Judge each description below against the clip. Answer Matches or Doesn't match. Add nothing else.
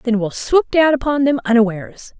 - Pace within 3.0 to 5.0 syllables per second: Doesn't match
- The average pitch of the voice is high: Matches